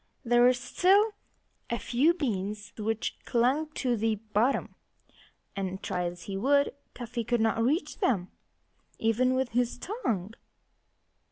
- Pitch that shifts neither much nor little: Yes, average, 3.8 semitones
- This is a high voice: Yes, high, 235 Hz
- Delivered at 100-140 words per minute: Yes, slow, 135 wpm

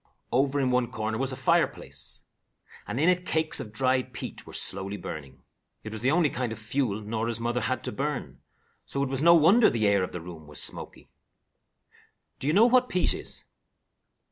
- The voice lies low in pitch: Yes, low, 125 Hz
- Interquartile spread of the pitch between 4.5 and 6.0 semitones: Yes, average, 5.1 semitones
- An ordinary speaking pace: Yes, average, 195 wpm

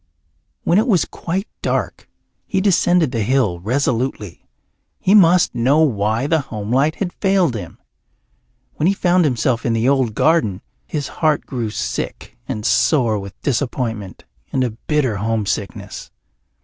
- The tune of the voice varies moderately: No, wide, 6.6 semitones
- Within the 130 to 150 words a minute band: Yes, average, 140 wpm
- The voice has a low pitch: Yes, low, 130 Hz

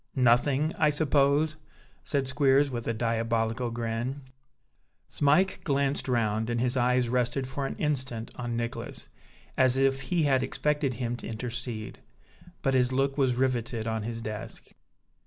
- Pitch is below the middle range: Yes, low, 125 Hz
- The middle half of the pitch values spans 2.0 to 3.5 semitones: Yes, average, 2.9 semitones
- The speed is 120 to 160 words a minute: Yes, average, 145 wpm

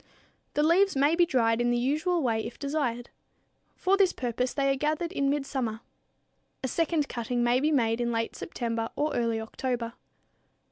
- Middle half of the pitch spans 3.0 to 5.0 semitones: Yes, average, 4.4 semitones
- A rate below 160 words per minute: No, average, 175 wpm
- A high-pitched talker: Yes, very high, 260 Hz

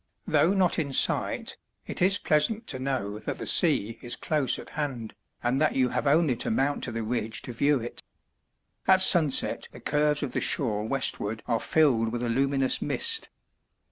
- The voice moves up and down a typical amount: Yes, average, 4.5 semitones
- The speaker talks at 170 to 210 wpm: Yes, average, 185 wpm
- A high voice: No, low, 135 Hz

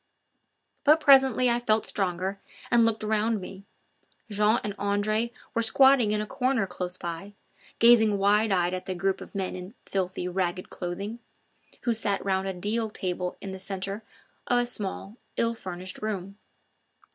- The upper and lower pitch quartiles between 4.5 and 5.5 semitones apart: No, average, 3.2 semitones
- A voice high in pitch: Yes, high, 205 Hz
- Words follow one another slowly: No, average, 165 wpm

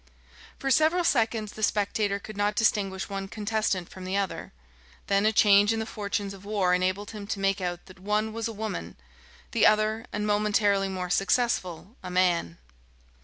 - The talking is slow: No, average, 175 wpm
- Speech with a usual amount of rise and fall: No, narrow, 2.0 semitones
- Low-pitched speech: No, high, 205 Hz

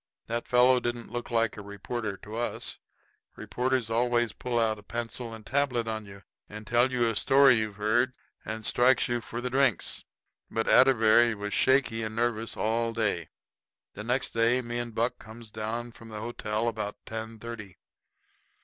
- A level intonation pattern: Yes, narrow, 1.8 semitones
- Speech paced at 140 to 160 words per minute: No, average, 175 wpm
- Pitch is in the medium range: No, low, 115 Hz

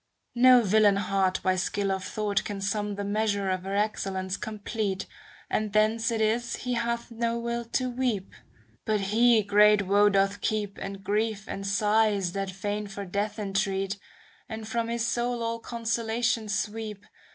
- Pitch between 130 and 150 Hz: No, high, 210 Hz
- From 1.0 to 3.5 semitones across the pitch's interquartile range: Yes, narrow, 2.5 semitones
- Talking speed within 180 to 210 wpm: No, average, 165 wpm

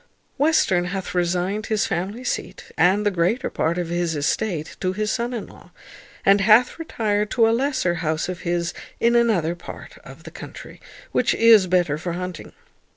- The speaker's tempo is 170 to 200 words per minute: Yes, average, 175 wpm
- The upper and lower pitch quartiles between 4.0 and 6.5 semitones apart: Yes, average, 4.3 semitones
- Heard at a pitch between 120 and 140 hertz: No, medium, 185 Hz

